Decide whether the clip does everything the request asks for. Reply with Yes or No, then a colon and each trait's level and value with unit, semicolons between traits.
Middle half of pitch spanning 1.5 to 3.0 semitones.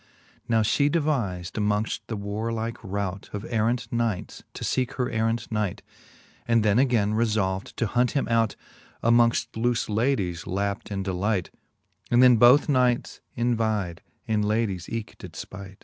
Yes: average, 2.7 semitones